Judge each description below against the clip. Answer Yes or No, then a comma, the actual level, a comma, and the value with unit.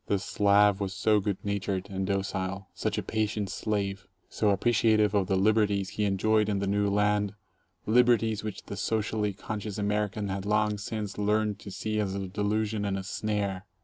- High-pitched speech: No, low, 105 Hz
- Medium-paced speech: Yes, average, 180 wpm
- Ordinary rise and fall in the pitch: No, narrow, 1.4 semitones